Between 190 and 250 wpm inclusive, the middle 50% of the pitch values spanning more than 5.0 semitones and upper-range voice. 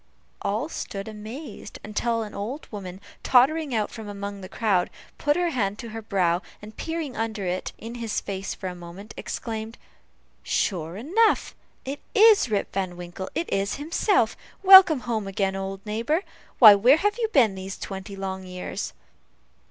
No: average, 165 wpm; wide, 5.4 semitones; high, 215 Hz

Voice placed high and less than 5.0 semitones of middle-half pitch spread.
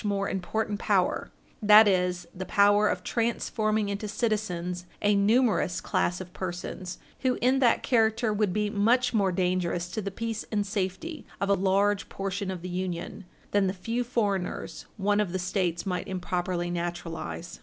Yes: high, 200 Hz; average, 3.0 semitones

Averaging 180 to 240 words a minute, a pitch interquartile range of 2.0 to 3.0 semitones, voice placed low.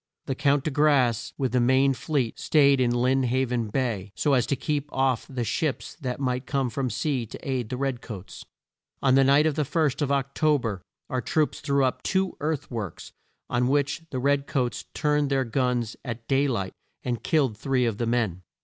Yes: fast, 205 wpm; narrow, 2.6 semitones; low, 130 Hz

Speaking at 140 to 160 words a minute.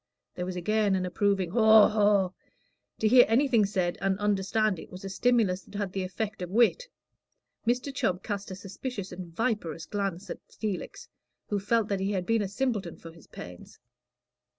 No: average, 180 wpm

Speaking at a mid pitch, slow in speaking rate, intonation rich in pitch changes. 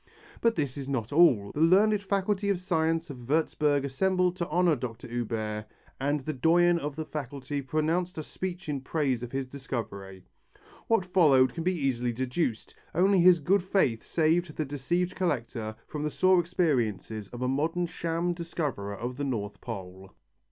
No: medium, 150 Hz; average, 170 wpm; wide, 5.8 semitones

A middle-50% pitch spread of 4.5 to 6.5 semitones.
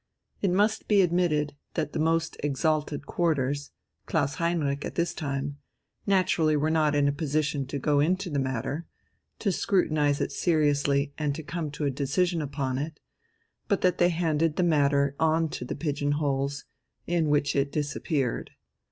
No: average, 2.7 semitones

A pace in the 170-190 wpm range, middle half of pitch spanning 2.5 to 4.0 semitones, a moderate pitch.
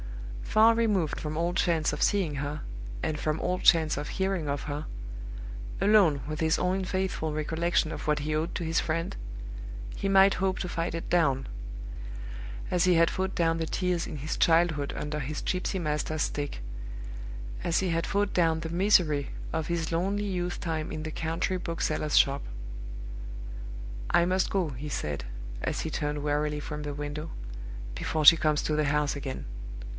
Yes: average, 175 wpm; average, 3.1 semitones; medium, 160 Hz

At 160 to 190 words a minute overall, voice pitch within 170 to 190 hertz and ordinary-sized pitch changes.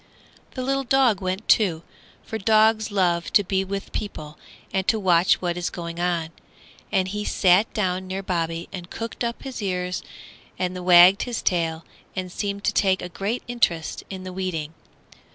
Yes: average, 170 wpm; medium, 185 Hz; average, 3.0 semitones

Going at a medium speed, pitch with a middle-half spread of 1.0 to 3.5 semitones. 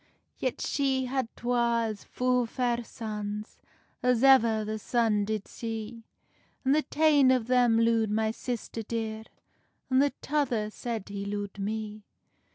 Yes: average, 145 wpm; average, 2.7 semitones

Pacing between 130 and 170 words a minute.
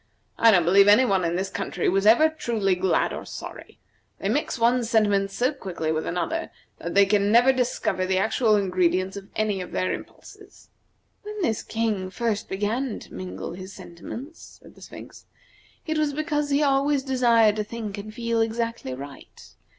No: average, 180 wpm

